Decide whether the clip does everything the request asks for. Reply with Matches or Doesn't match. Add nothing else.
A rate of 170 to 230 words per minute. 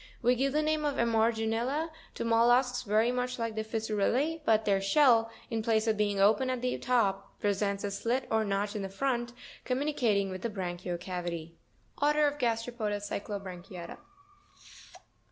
Doesn't match